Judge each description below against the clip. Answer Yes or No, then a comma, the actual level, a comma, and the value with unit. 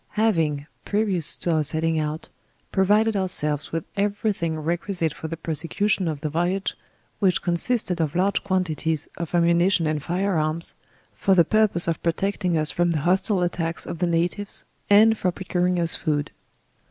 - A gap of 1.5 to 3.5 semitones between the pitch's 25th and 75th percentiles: Yes, average, 3.2 semitones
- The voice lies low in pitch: No, medium, 175 Hz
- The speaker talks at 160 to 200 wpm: Yes, average, 175 wpm